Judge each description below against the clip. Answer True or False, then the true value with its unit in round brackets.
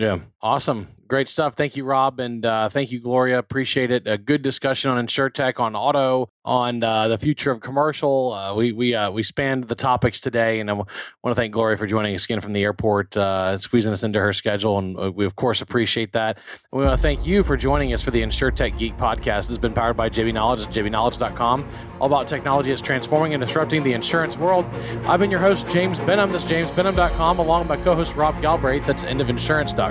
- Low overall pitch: True (125 Hz)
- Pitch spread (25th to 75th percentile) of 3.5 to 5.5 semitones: True (4.2 semitones)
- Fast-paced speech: True (230 wpm)